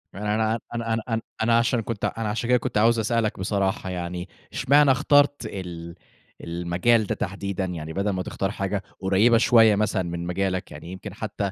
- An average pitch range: Yes, average, 3.5 semitones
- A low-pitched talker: Yes, low, 100 Hz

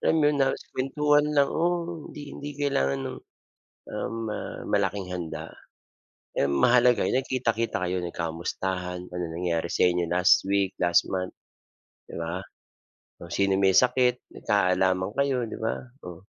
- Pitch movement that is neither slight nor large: No, wide, 6.7 semitones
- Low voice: Yes, very low, 95 Hz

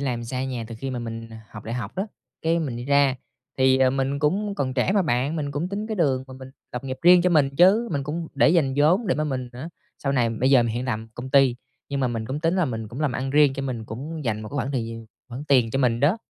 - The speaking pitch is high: No, low, 135 Hz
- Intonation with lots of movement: No, average, 3.7 semitones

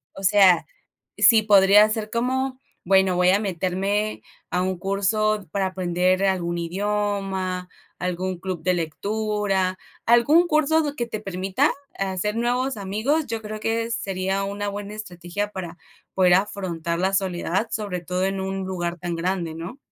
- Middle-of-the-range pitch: No, high, 195 Hz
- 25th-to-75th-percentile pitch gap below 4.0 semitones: Yes, narrow, 2.6 semitones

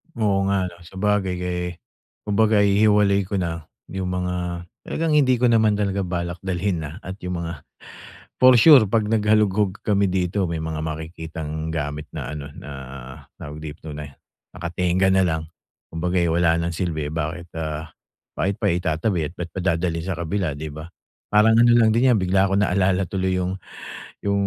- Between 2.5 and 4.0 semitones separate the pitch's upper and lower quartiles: Yes, average, 3.5 semitones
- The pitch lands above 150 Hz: No, very low, 90 Hz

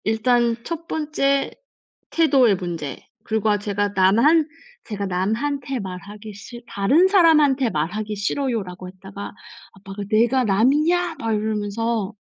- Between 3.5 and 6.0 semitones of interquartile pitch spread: Yes, wide, 5.6 semitones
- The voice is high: Yes, high, 220 Hz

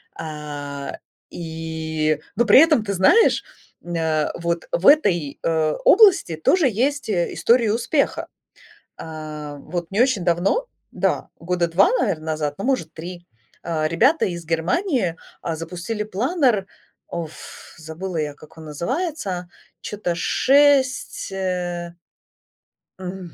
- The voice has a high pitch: No, medium, 175 Hz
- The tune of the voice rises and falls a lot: Yes, wide, 6.0 semitones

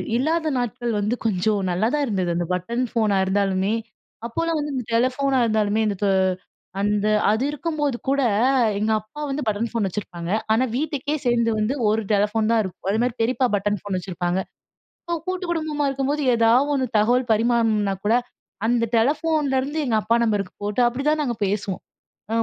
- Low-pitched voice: No, high, 230 Hz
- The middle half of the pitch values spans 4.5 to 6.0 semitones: Yes, average, 4.8 semitones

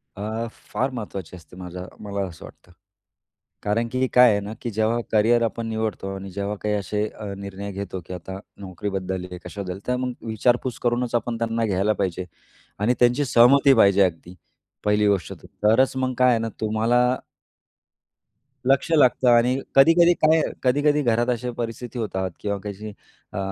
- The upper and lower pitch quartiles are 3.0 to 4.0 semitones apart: Yes, average, 3.7 semitones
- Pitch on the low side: Yes, low, 110 Hz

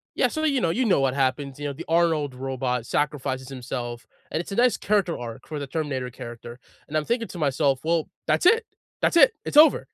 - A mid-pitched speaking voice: Yes, medium, 145 Hz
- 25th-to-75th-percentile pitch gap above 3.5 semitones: Yes, average, 5.1 semitones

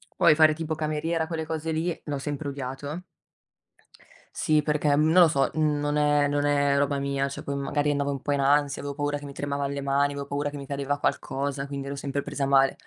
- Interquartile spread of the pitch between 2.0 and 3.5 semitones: No, narrow, 1.3 semitones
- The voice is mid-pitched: Yes, medium, 145 Hz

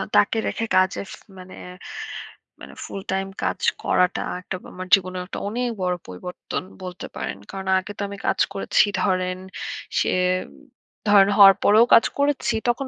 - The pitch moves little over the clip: Yes, narrow, 2.2 semitones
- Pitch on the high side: Yes, high, 195 Hz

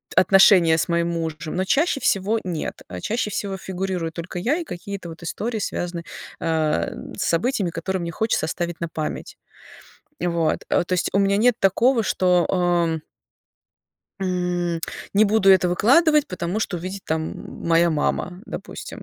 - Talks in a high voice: No, medium, 180 Hz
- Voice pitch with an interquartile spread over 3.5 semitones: No, average, 2.9 semitones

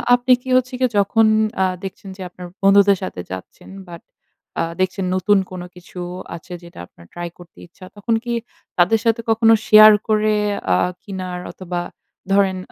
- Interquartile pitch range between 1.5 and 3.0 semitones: No, average, 3.4 semitones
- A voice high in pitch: Yes, high, 195 Hz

